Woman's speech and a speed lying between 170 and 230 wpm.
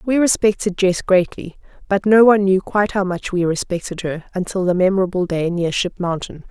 Yes: female; average, 195 wpm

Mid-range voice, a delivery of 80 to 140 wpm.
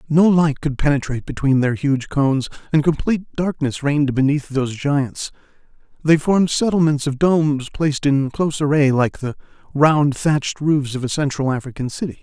No: medium, 145 Hz; average, 165 wpm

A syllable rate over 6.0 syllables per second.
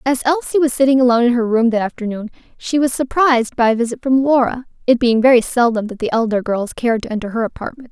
Yes: 6.5 syllables/s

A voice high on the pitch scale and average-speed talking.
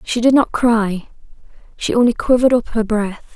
Yes: high, 230 Hz; average, 160 wpm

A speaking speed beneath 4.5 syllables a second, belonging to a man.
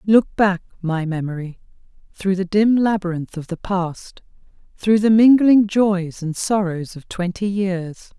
No: 4.0 syllables/s; female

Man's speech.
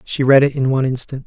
Yes: male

